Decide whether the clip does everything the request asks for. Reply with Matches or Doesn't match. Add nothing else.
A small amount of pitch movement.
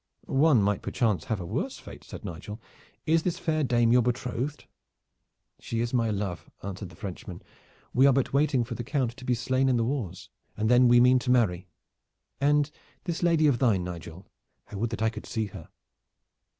Doesn't match